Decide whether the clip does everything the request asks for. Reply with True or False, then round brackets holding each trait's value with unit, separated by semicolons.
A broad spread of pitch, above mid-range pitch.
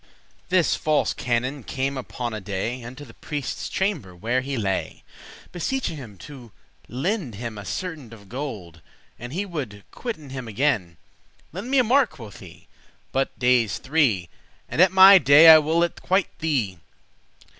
False (6.3 semitones; 135 Hz)